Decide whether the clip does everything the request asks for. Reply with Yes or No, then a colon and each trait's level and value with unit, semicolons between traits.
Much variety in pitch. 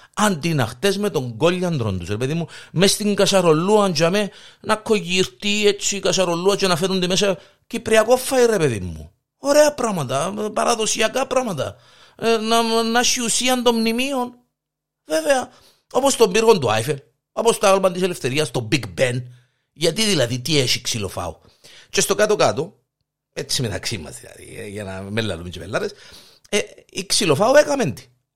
Yes: wide, 8.4 semitones